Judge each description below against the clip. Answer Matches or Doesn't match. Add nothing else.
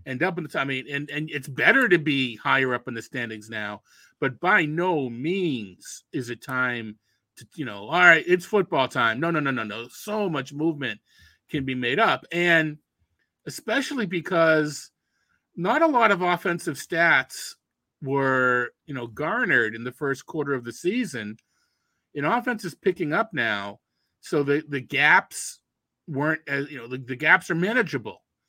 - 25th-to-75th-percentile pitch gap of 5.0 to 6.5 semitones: Matches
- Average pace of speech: Matches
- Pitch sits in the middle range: Matches